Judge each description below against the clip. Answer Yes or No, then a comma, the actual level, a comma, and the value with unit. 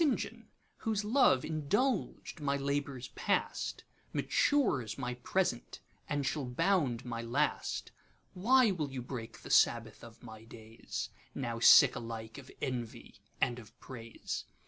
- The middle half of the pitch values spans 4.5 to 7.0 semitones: Yes, average, 5.2 semitones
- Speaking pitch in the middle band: No, low, 130 Hz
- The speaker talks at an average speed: No, slow, 120 wpm